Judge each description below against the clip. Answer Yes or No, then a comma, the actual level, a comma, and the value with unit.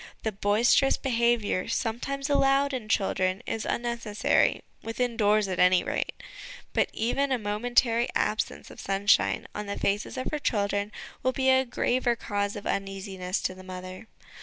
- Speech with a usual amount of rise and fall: Yes, average, 3.5 semitones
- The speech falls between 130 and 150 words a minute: No, average, 160 wpm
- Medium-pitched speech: No, high, 220 Hz